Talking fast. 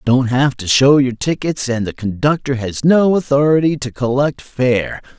No: average, 175 wpm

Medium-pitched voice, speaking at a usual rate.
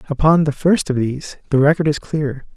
No: medium, 145 Hz; fast, 210 wpm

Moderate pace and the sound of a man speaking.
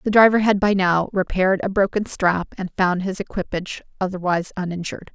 No: average, 175 wpm; female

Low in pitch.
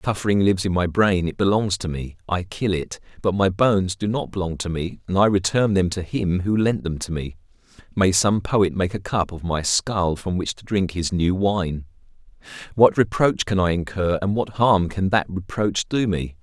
Yes: very low, 95 Hz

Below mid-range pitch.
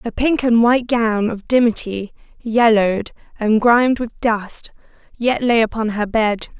No: high, 225 Hz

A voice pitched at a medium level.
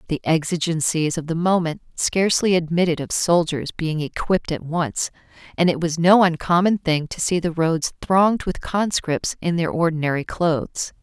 Yes: medium, 165 Hz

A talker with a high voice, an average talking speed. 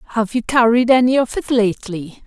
Yes: high, 230 Hz; average, 185 wpm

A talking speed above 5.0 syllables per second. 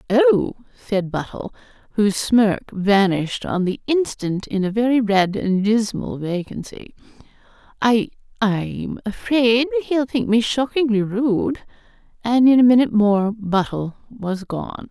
No: 4.0 syllables/s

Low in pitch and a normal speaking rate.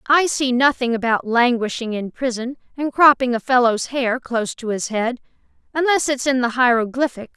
No: very high, 250 Hz; average, 170 wpm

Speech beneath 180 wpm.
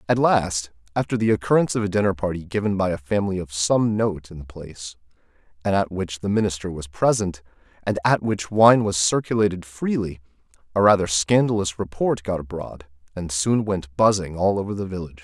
No: average, 185 wpm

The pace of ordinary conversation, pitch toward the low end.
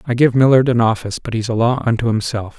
No: fast, 255 wpm; low, 120 Hz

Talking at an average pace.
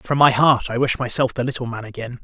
No: fast, 270 wpm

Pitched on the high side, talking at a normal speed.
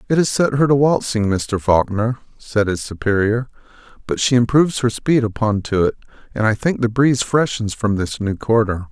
No: low, 115 Hz; average, 195 wpm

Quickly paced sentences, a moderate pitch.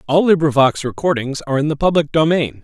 No: average, 180 wpm; medium, 150 Hz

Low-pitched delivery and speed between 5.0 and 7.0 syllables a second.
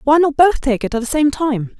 No: very high, 280 Hz; 5.3 syllables/s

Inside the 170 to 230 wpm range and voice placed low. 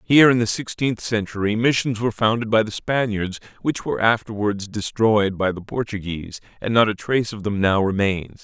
Yes: average, 185 wpm; low, 110 Hz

